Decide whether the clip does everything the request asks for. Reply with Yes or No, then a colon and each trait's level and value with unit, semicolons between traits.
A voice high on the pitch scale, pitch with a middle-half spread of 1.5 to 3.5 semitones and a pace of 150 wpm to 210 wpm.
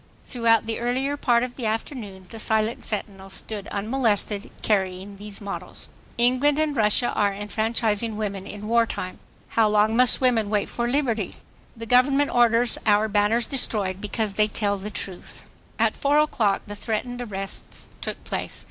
Yes: high, 220 Hz; average, 2.8 semitones; average, 160 wpm